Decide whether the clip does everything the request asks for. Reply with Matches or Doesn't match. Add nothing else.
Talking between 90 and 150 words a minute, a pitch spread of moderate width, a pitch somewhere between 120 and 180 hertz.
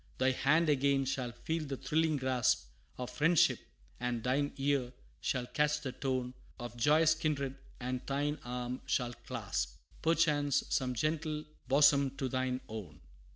Matches